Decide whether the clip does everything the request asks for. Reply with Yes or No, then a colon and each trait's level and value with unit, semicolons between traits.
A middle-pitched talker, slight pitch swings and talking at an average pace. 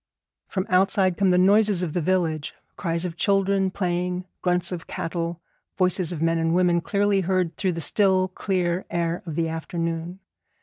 Yes: medium, 180 Hz; narrow, 2.0 semitones; average, 170 wpm